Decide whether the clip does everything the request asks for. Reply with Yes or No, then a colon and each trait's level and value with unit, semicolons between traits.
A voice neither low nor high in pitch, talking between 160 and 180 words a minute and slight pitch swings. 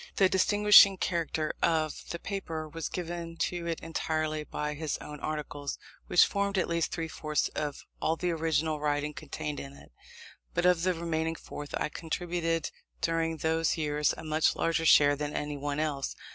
Yes: medium, 160 Hz; average, 170 wpm; narrow, 2.0 semitones